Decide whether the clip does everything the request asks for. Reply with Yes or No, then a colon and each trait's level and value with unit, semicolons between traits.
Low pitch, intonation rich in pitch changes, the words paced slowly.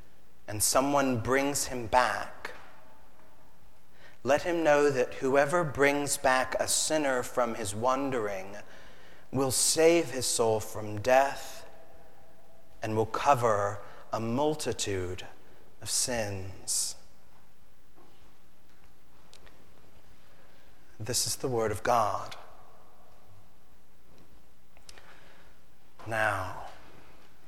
Yes: low, 125 Hz; wide, 5.9 semitones; slow, 80 wpm